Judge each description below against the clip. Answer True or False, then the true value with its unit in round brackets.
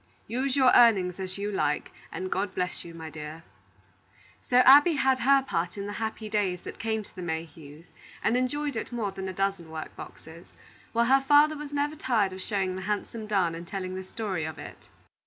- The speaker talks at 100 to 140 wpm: False (205 wpm)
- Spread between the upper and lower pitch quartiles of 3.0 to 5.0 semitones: False (5.5 semitones)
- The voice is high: True (200 Hz)